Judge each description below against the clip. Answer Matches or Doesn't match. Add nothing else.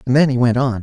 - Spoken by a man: Matches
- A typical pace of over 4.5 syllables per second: Matches